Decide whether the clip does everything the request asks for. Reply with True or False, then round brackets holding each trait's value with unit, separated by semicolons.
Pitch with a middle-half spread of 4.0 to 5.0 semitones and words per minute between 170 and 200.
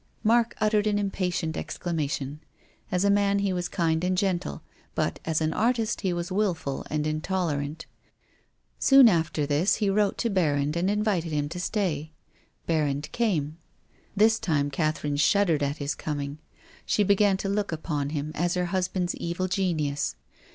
False (4.7 semitones; 160 wpm)